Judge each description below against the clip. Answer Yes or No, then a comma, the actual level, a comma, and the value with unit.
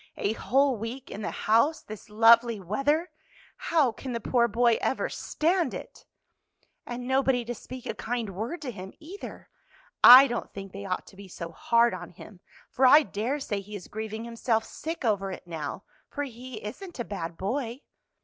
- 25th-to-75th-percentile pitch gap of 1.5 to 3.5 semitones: No, average, 4.5 semitones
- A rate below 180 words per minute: No, average, 185 wpm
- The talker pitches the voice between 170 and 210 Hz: No, high, 235 Hz